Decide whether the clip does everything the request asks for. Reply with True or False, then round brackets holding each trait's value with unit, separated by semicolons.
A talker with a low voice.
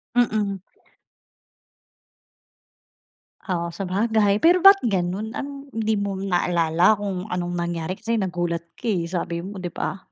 False (195 Hz)